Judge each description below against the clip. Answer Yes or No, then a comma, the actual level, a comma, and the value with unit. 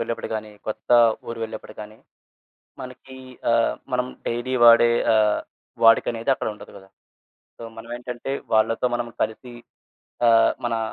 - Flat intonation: Yes, narrow, 1.5 semitones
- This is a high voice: No, low, 115 Hz